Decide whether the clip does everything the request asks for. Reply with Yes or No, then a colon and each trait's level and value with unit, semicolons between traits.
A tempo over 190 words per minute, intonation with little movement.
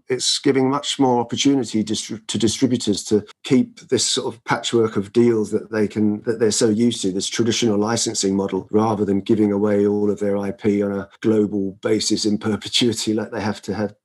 Yes: average, 200 wpm; narrow, 2.2 semitones